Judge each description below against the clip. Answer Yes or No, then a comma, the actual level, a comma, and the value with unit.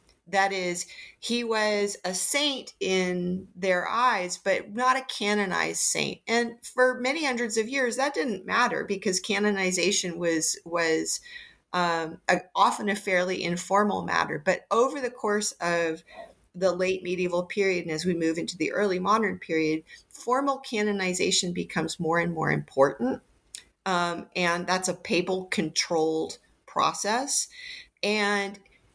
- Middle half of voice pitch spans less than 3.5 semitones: No, average, 3.8 semitones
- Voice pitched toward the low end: No, high, 190 Hz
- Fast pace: No, average, 140 wpm